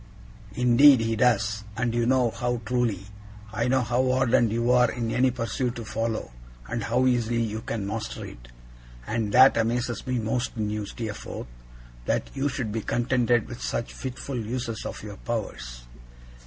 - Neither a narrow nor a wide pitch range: No, narrow, 2.1 semitones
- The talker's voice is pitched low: Yes, low, 115 Hz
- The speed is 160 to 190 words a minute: Yes, average, 170 wpm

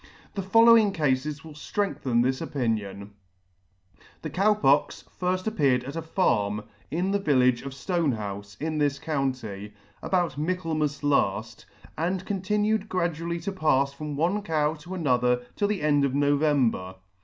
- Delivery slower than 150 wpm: Yes, average, 140 wpm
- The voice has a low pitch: No, medium, 150 Hz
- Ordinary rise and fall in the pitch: No, wide, 5.8 semitones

